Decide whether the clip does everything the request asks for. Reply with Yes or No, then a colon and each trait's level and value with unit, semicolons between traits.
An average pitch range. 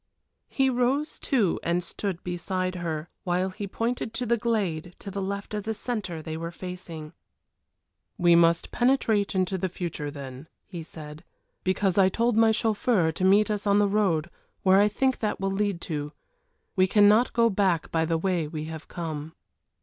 Yes: average, 4.1 semitones